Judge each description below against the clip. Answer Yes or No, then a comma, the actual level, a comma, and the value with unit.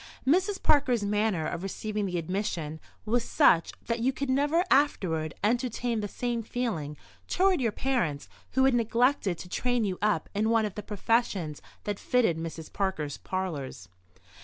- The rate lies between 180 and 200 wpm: No, average, 160 wpm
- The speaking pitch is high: Yes, high, 215 Hz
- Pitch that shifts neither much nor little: No, wide, 5.8 semitones